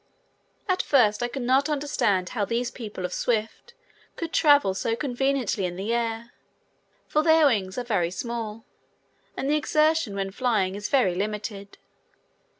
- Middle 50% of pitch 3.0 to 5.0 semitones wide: No, wide, 5.4 semitones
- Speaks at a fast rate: No, average, 150 wpm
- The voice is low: No, high, 235 Hz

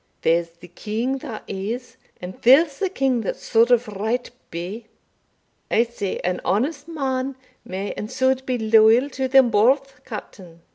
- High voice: Yes, high, 235 Hz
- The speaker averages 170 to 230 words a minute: No, average, 155 wpm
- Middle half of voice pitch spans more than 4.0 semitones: Yes, average, 4.4 semitones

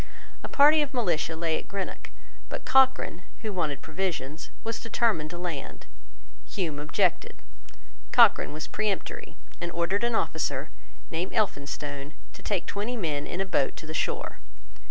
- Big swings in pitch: Yes, wide, 5.7 semitones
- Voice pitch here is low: No, medium, 175 Hz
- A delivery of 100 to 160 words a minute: Yes, average, 150 wpm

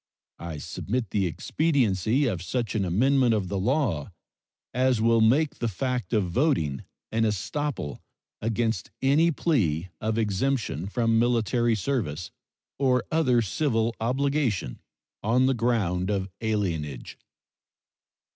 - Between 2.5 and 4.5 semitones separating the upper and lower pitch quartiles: No, average, 5.3 semitones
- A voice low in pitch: Yes, low, 115 Hz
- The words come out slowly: Yes, slow, 120 wpm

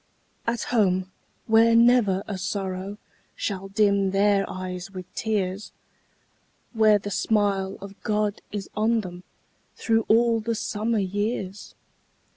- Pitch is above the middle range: Yes, high, 205 Hz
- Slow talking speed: Yes, slow, 120 wpm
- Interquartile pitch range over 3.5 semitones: No, narrow, 2.4 semitones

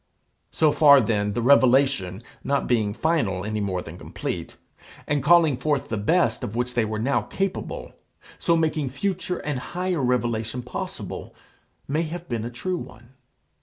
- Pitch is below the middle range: Yes, low, 130 Hz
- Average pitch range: No, wide, 5.9 semitones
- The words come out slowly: No, average, 160 wpm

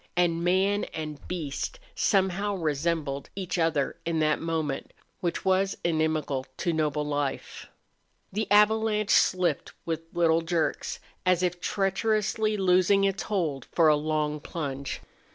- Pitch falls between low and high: Yes, medium, 170 Hz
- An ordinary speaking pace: No, slow, 130 wpm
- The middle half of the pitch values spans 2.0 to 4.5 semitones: Yes, average, 3.9 semitones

